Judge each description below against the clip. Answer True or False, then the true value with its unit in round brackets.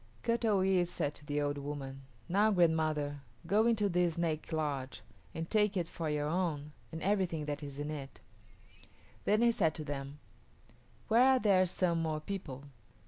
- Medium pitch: True (165 Hz)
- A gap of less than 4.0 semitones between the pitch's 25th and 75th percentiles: False (4.7 semitones)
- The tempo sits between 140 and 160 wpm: False (175 wpm)